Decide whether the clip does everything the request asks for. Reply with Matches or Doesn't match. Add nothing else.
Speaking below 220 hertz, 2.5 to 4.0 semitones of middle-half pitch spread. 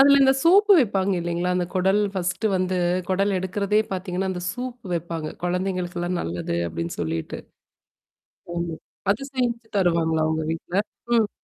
Matches